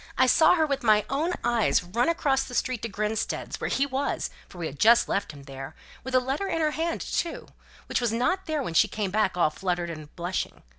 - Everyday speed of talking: No, fast, 235 wpm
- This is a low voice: No, high, 235 Hz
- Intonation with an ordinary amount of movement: No, wide, 7.3 semitones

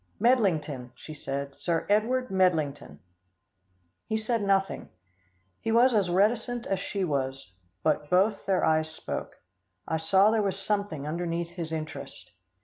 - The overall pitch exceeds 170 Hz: Yes, medium, 185 Hz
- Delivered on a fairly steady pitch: No, average, 5.1 semitones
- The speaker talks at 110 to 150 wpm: Yes, average, 140 wpm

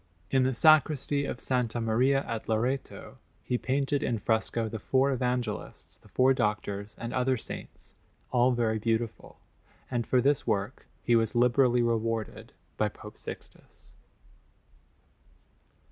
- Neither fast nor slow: No, slow, 130 wpm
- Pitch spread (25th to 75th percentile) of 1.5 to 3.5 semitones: Yes, narrow, 2.6 semitones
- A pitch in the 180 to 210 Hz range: No, low, 120 Hz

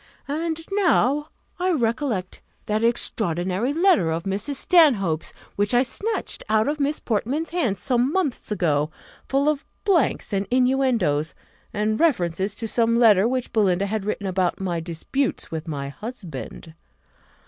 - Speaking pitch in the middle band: No, high, 225 Hz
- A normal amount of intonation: No, wide, 7.0 semitones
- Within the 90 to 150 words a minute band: Yes, average, 140 wpm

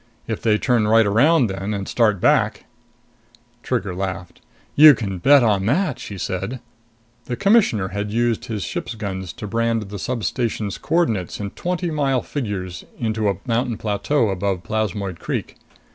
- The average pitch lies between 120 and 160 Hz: No, low, 110 Hz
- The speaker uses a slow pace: No, average, 160 wpm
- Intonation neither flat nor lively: Yes, average, 3.6 semitones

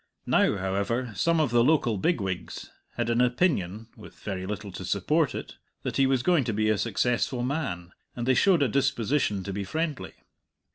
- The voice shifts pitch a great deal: Yes, wide, 5.7 semitones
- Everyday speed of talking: Yes, average, 185 wpm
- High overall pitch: No, low, 120 Hz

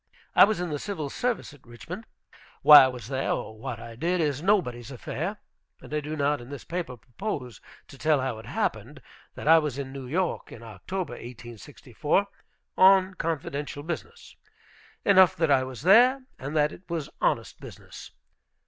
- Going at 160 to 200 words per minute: Yes, average, 175 wpm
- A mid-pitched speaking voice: Yes, medium, 150 Hz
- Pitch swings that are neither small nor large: No, wide, 5.8 semitones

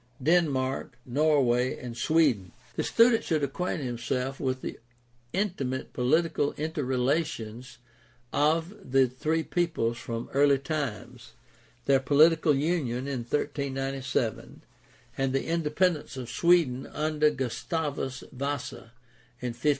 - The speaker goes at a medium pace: No, slow, 110 wpm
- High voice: No, medium, 140 Hz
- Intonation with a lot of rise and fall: No, average, 3.7 semitones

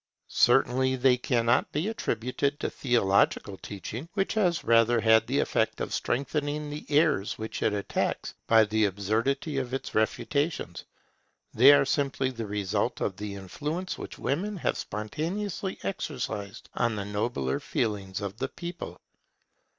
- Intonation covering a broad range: Yes, wide, 5.7 semitones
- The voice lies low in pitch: Yes, low, 125 Hz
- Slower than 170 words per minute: Yes, average, 145 wpm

